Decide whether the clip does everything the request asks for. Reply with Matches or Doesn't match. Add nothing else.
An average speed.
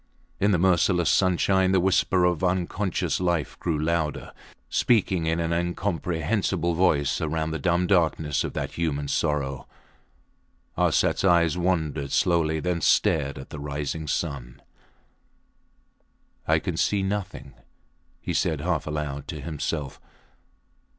Doesn't match